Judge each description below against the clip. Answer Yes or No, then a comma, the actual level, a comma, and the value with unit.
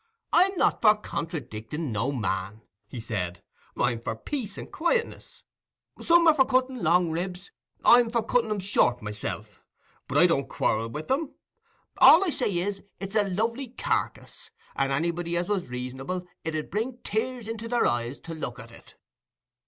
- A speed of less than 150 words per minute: No, average, 160 wpm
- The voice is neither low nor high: Yes, medium, 180 Hz